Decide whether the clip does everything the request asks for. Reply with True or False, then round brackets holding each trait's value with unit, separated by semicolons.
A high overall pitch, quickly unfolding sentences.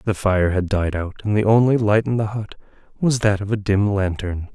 False (105 Hz; 235 wpm)